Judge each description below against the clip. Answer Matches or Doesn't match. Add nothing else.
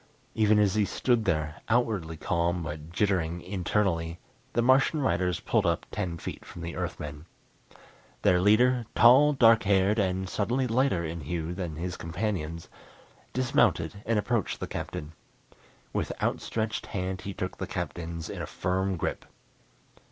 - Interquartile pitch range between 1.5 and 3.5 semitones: Doesn't match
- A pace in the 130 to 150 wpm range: Matches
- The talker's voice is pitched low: Matches